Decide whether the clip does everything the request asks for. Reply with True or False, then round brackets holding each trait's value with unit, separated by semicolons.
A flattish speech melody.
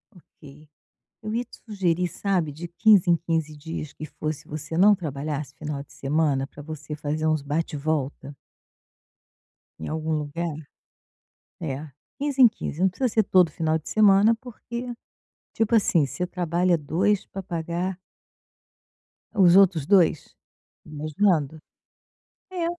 False (4.3 semitones)